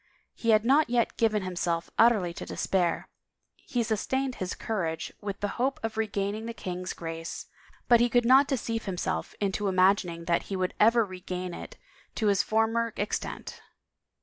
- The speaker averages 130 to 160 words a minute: No, average, 170 wpm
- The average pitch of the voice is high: Yes, high, 205 Hz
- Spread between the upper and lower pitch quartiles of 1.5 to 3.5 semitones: No, average, 4.1 semitones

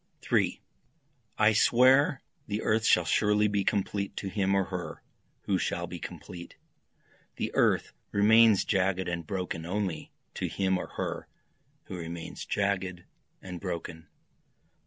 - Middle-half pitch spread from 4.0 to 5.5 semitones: No, average, 2.9 semitones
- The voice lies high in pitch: No, very low, 95 Hz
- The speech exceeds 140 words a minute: No, slow, 135 wpm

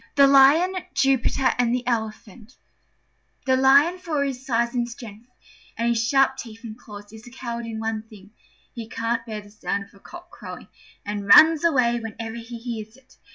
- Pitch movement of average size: Yes, average, 3.2 semitones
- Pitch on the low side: No, high, 235 Hz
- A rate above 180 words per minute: Yes, average, 190 wpm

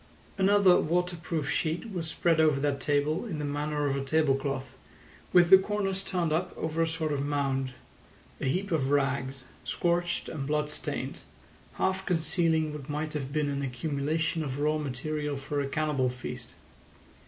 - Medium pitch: Yes, medium, 150 Hz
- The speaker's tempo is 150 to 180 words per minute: Yes, average, 160 wpm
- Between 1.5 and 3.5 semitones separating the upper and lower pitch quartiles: Yes, average, 3.1 semitones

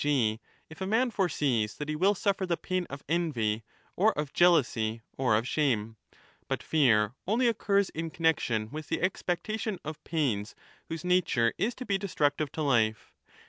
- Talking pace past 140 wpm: Yes, average, 175 wpm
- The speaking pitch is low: No, medium, 155 Hz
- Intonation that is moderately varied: No, wide, 7.7 semitones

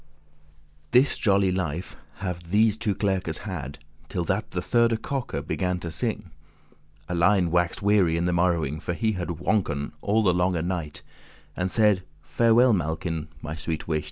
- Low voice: Yes, very low, 90 Hz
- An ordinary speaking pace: Yes, average, 160 wpm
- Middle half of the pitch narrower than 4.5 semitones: Yes, average, 3.6 semitones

